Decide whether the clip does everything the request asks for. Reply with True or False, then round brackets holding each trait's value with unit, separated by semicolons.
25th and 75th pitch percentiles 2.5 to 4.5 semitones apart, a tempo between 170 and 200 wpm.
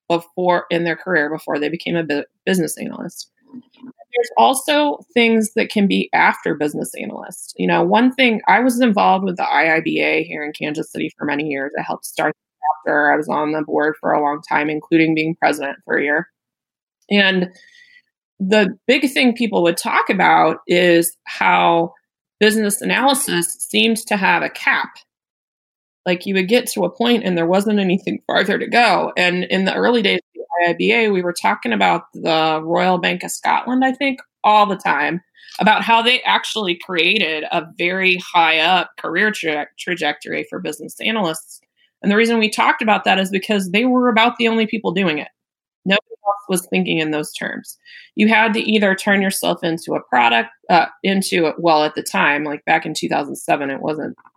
False (5.3 semitones; 185 wpm)